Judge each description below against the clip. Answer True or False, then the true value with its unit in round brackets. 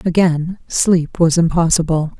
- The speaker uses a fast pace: False (110 wpm)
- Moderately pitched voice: True (165 Hz)